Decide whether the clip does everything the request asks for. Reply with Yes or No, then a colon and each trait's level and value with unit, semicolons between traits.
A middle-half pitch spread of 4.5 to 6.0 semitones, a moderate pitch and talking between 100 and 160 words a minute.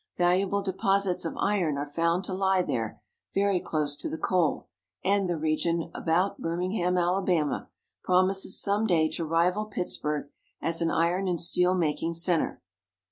No: narrow, 2.5 semitones; medium, 180 Hz; average, 150 wpm